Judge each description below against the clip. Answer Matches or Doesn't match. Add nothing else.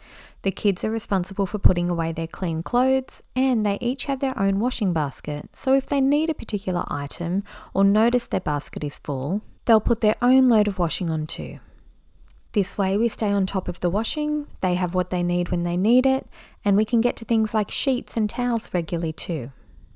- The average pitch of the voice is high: Matches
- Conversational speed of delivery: Doesn't match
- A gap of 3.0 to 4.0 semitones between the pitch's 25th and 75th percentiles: Doesn't match